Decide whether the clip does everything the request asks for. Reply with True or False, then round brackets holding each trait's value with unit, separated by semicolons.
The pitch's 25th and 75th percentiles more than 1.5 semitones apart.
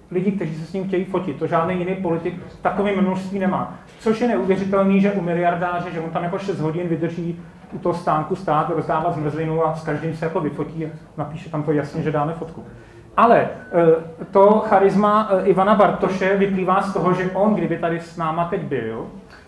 True (2.7 semitones)